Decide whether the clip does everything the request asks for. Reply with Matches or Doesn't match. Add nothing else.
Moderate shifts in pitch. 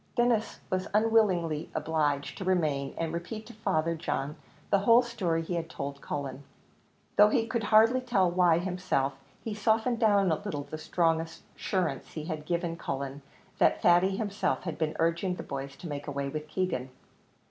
Matches